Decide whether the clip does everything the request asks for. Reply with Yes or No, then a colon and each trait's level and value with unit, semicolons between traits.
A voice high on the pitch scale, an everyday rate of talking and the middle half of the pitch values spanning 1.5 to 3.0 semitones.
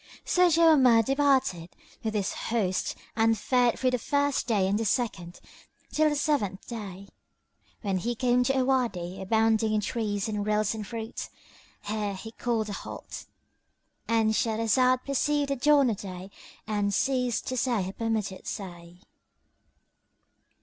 No: high, 225 Hz; average, 150 wpm; average, 4.0 semitones